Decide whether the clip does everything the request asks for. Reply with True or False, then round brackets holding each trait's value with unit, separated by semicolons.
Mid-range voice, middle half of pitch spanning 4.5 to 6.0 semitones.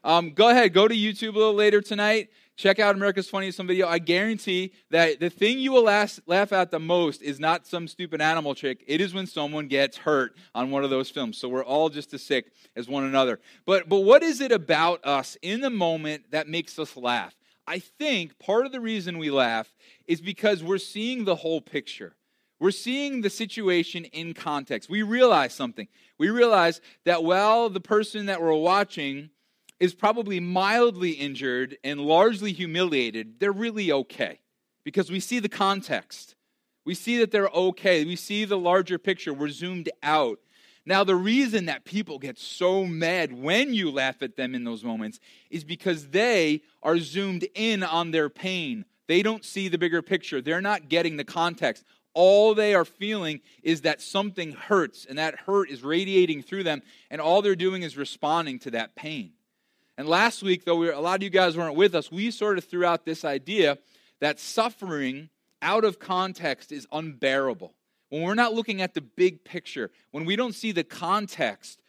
True (180 Hz; 4.9 semitones)